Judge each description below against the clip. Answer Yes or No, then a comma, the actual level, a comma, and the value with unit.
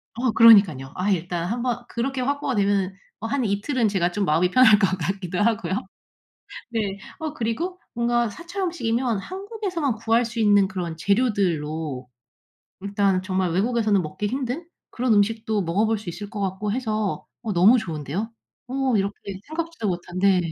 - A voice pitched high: Yes, high, 215 Hz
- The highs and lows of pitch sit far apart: No, average, 4.4 semitones